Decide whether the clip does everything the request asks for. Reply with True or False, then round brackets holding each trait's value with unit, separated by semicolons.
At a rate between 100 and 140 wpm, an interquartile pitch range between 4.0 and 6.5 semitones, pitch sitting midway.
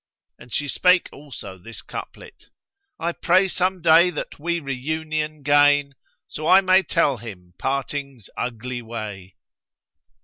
True (135 wpm; 5.3 semitones; 145 Hz)